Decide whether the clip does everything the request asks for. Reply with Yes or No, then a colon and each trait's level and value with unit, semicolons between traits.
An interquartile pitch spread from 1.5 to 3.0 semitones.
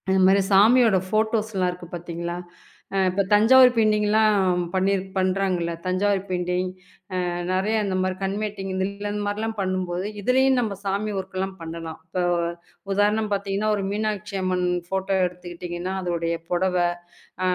Yes: narrow, 2.4 semitones